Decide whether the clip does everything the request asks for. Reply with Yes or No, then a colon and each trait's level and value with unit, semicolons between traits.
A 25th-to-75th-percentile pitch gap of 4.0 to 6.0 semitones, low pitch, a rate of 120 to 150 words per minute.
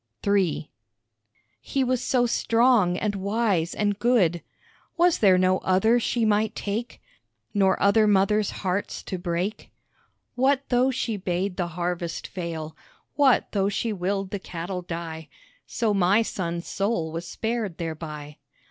No: average, 4.3 semitones; high, 195 Hz; average, 140 wpm